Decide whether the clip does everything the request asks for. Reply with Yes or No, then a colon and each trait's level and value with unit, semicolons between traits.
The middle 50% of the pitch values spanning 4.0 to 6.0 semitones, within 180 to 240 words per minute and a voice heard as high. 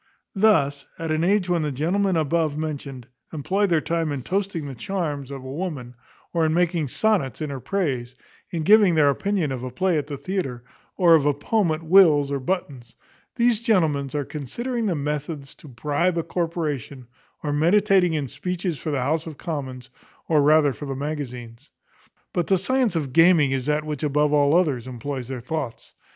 No: average, 4.3 semitones; average, 185 wpm; medium, 155 Hz